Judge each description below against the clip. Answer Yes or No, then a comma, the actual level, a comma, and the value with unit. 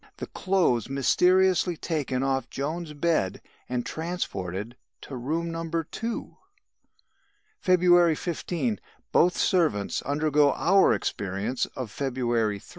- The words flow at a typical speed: No, slow, 110 wpm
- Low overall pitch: No, medium, 150 Hz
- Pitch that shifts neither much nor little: No, wide, 6.0 semitones